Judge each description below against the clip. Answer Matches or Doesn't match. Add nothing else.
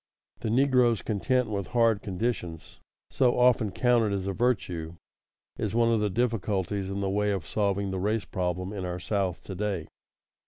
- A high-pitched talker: Doesn't match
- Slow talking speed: Doesn't match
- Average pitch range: Matches